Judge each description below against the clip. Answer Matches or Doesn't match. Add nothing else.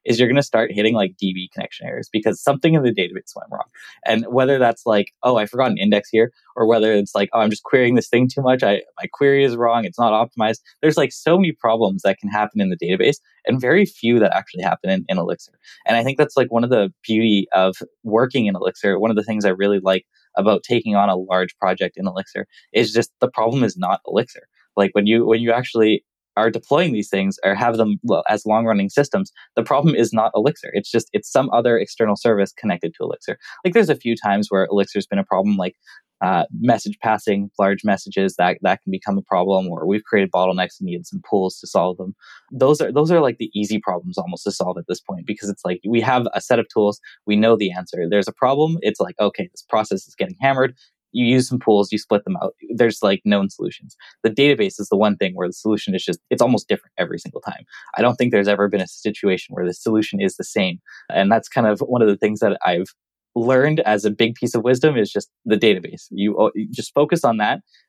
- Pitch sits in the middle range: Doesn't match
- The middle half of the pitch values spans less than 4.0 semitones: Doesn't match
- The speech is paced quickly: Matches